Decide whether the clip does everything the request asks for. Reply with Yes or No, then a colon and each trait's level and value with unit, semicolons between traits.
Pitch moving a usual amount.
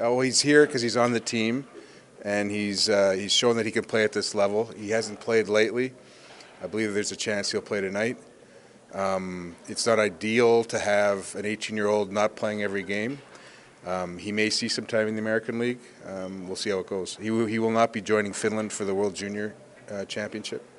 No: narrow, 2.1 semitones